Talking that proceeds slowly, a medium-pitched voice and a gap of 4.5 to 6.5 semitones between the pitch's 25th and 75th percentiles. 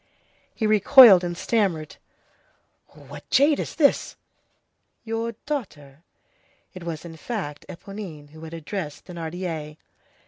Yes: slow, 110 wpm; medium, 175 Hz; wide, 5.6 semitones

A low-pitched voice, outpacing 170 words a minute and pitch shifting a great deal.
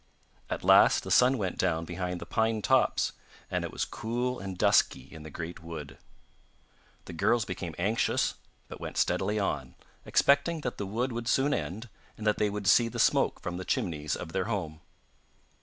Yes: low, 100 Hz; average, 185 wpm; wide, 5.7 semitones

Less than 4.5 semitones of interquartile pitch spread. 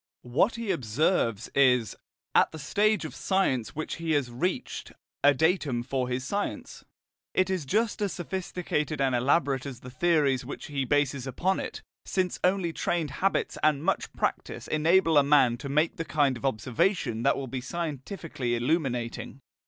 No: average, 5.2 semitones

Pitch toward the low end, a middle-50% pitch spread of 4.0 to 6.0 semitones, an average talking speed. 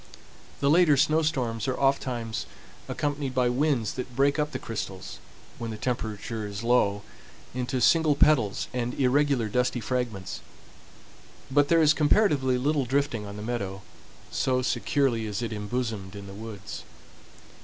Yes: low, 125 Hz; average, 4.3 semitones; average, 145 wpm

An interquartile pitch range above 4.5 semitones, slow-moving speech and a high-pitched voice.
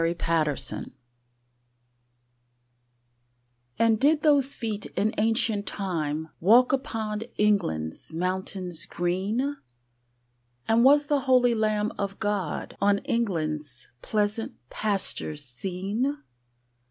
Yes: average, 5.0 semitones; slow, 95 wpm; high, 205 Hz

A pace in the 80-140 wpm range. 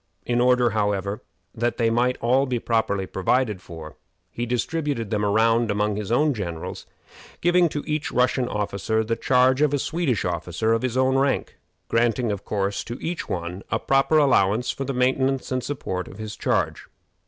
No: average, 175 wpm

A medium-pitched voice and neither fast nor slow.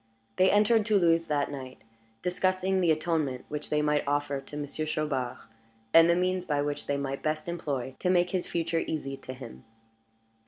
Yes: medium, 155 Hz; average, 170 wpm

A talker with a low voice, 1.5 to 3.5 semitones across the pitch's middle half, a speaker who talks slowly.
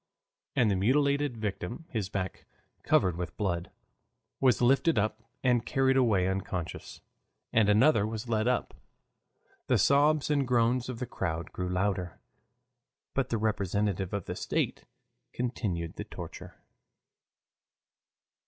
No: low, 110 Hz; average, 4.9 semitones; slow, 125 wpm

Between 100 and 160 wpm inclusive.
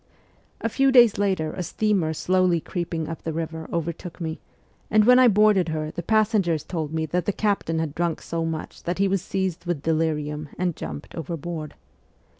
No: average, 185 wpm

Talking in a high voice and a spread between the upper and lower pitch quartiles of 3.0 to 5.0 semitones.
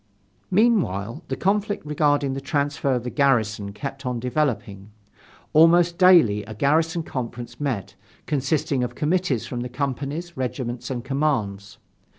No: low, 135 Hz; average, 4.3 semitones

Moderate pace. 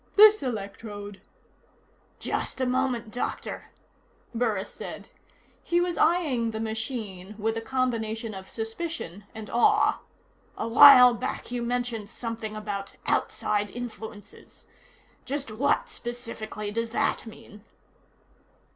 No: slow, 115 wpm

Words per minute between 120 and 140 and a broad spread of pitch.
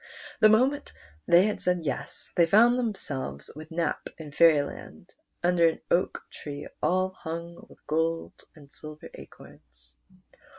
No: slow, 135 wpm; average, 3.9 semitones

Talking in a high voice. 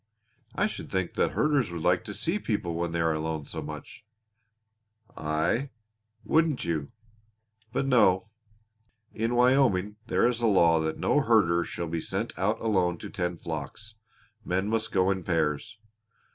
No: very low, 95 Hz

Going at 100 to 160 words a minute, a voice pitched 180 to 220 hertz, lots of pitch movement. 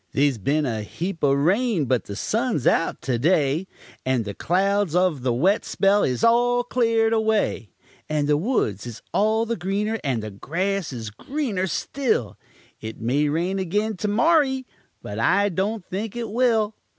No: average, 170 wpm; medium, 185 Hz; wide, 8.2 semitones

